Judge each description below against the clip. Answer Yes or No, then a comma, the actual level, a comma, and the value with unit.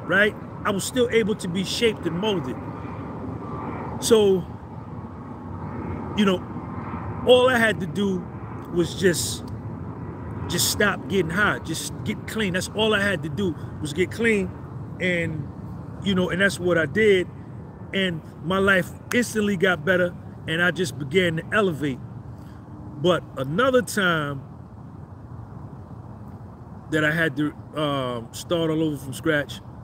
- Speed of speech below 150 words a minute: Yes, average, 140 wpm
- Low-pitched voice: No, medium, 155 Hz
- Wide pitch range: Yes, wide, 7.5 semitones